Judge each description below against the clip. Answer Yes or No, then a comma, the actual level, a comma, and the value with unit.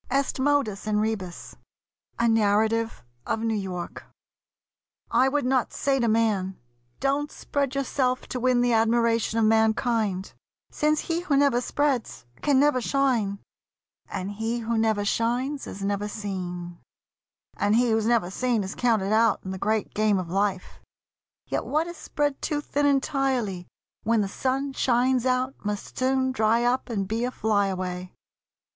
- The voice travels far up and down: No, average, 4.2 semitones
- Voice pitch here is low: No, high, 230 Hz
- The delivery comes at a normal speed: Yes, average, 155 wpm